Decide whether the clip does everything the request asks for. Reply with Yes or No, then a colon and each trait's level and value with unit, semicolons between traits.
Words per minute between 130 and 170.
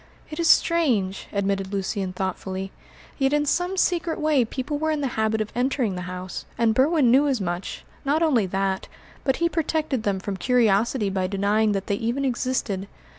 No: average, 180 wpm